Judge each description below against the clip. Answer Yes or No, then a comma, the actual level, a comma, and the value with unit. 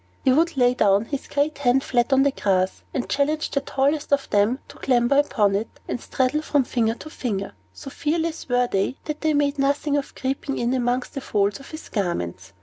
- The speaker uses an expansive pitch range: No, average, 3.9 semitones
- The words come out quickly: Yes, fast, 210 wpm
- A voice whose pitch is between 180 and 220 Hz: No, very high, 265 Hz